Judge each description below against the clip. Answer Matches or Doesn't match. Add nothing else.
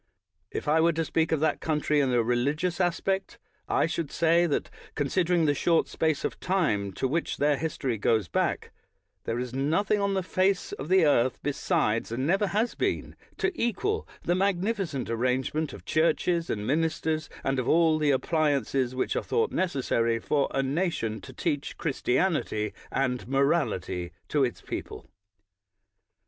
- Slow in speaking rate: Doesn't match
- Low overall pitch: Doesn't match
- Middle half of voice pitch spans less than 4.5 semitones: Doesn't match